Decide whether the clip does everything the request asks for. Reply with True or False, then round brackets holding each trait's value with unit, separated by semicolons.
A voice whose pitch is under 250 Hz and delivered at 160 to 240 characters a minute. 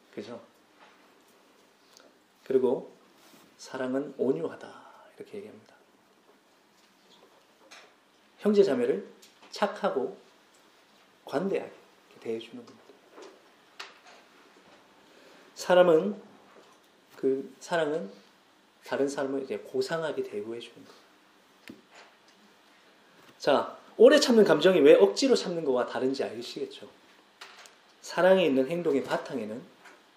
True (185 Hz; 205 characters per minute)